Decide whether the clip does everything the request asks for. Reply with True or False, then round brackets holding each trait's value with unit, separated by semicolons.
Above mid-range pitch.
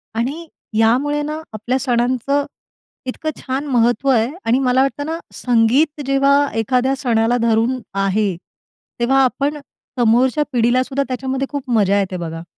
True (255 Hz)